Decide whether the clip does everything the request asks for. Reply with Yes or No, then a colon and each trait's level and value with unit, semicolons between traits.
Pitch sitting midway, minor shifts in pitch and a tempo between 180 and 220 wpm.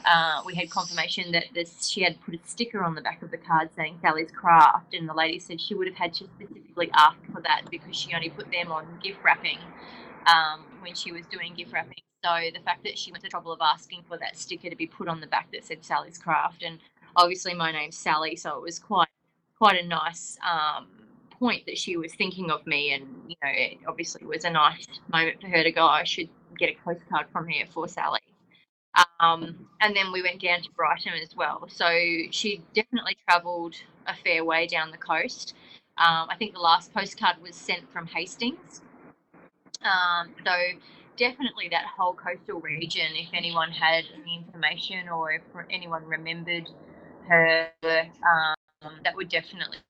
Yes: medium, 170 Hz; narrow, 1.8 semitones; average, 200 wpm